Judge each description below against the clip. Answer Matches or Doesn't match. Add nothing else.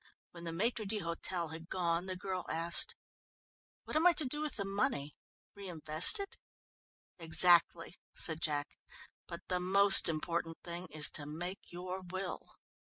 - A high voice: Doesn't match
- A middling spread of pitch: Matches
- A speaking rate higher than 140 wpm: Matches